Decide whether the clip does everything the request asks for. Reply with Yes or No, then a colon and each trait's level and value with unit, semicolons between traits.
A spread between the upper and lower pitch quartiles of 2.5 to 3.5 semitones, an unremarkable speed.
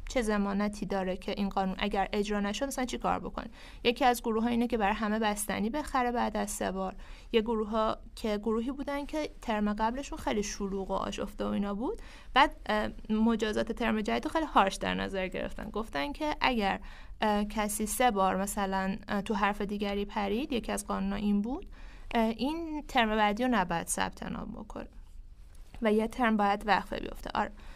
No: average, 3.0 semitones; fast, 180 wpm